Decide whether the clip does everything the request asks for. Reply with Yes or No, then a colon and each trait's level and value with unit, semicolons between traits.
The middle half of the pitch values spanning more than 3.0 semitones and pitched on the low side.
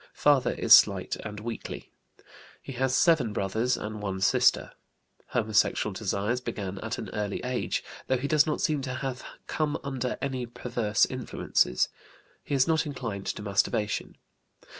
Yes: average, 4.1 semitones; low, 120 Hz